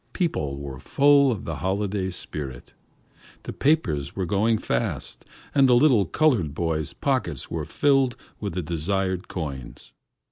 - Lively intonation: Yes, wide, 8.3 semitones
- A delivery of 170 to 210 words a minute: No, average, 140 wpm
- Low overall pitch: Yes, very low, 95 Hz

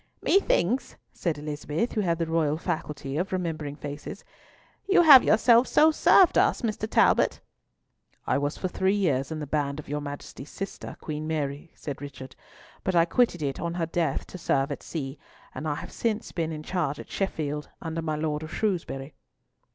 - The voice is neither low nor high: Yes, medium, 160 Hz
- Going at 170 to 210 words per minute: Yes, average, 180 wpm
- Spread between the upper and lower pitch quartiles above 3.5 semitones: Yes, average, 4.0 semitones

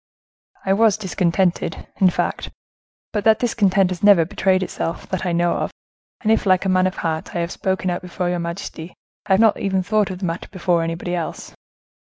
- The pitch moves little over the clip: Yes, narrow, 2.2 semitones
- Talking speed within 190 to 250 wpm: Yes, fast, 205 wpm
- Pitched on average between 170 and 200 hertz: Yes, medium, 185 Hz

